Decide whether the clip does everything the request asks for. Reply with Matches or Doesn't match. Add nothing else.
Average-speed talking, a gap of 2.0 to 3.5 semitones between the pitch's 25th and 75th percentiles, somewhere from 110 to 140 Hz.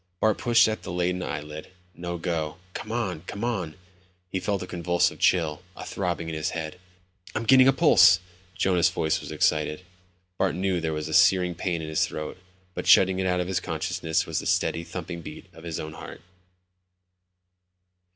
Doesn't match